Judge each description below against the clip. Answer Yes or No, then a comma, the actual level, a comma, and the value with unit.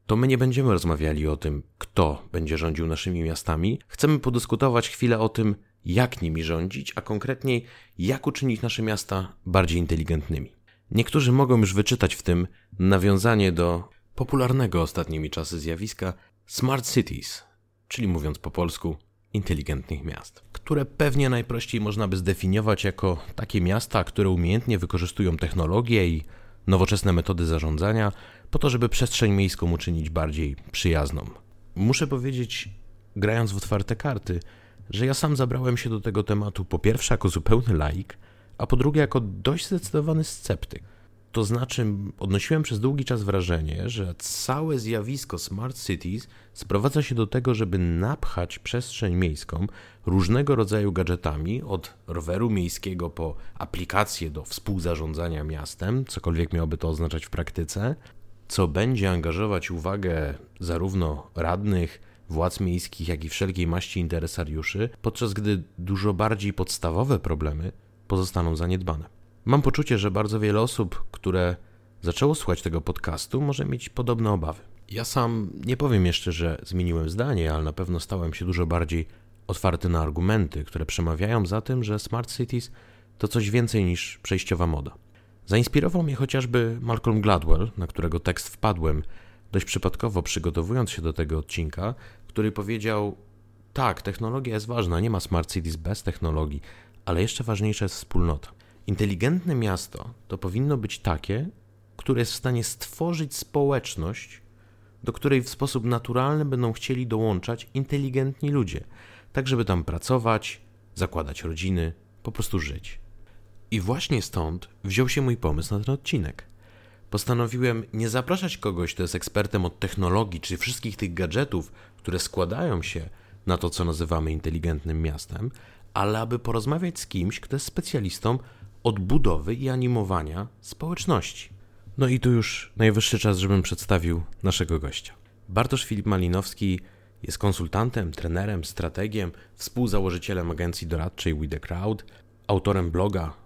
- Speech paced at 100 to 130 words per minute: No, average, 140 wpm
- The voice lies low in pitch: Yes, low, 100 Hz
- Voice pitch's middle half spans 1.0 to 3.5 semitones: No, average, 4.6 semitones